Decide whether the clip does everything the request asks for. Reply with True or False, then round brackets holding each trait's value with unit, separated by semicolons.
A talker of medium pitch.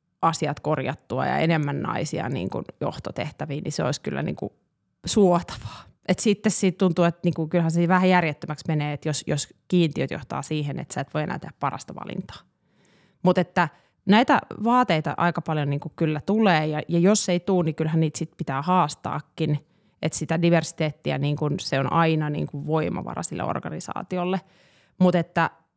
True (165 Hz)